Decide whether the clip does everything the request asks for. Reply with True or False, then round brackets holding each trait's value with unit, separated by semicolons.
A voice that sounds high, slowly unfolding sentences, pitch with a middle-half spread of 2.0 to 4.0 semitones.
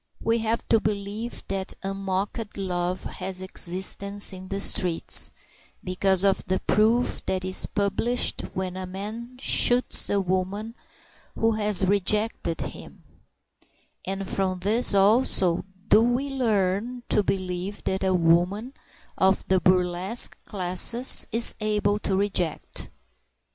True (195 Hz; 125 wpm; 2.6 semitones)